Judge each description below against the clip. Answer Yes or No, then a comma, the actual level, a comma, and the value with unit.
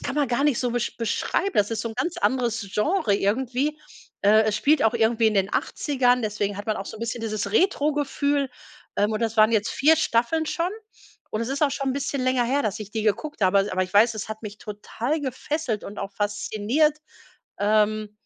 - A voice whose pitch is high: Yes, high, 230 Hz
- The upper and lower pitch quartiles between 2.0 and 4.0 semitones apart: No, average, 4.8 semitones